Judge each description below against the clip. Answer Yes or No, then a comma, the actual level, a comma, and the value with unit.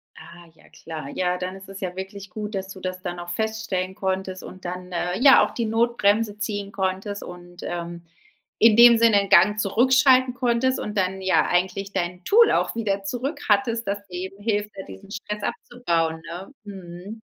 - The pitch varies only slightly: No, average, 3.2 semitones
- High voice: Yes, high, 195 Hz